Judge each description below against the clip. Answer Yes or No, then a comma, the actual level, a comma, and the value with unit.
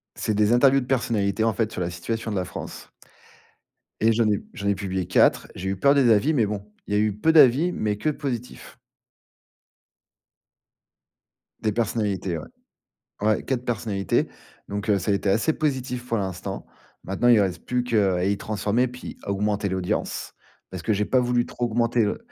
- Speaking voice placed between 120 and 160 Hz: No, low, 110 Hz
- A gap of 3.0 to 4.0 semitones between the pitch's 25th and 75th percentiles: Yes, average, 3.6 semitones